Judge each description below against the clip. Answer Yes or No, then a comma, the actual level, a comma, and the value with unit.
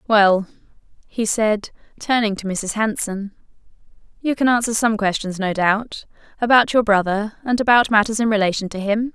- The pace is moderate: Yes, average, 155 wpm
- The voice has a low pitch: No, high, 215 Hz